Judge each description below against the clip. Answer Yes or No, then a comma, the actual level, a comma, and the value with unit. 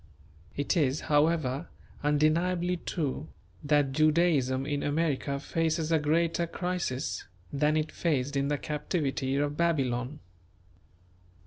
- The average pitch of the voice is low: No, medium, 150 Hz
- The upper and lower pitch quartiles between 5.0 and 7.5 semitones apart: No, average, 2.9 semitones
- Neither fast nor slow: No, slow, 110 wpm